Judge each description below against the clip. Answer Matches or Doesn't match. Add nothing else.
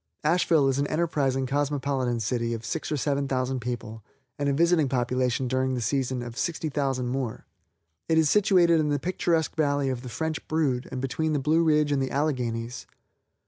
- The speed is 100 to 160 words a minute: Doesn't match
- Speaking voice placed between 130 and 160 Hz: Matches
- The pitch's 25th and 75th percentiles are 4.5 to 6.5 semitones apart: Doesn't match